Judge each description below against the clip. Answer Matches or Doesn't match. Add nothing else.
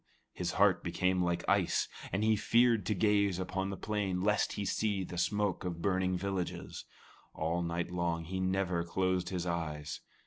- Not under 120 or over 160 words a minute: Doesn't match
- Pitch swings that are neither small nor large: Doesn't match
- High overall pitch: Doesn't match